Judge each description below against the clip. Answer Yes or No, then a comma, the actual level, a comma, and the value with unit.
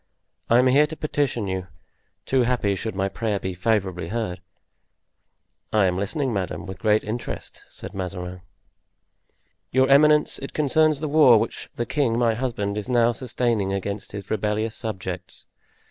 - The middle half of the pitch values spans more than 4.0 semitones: Yes, average, 4.7 semitones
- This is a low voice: Yes, low, 110 Hz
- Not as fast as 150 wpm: No, average, 160 wpm